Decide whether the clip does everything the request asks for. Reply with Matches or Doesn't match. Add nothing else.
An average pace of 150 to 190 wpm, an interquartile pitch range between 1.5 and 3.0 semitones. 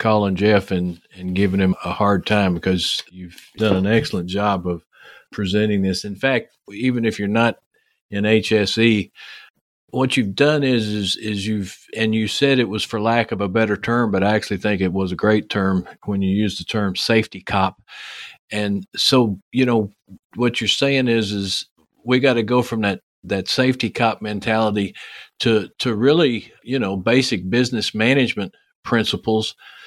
Matches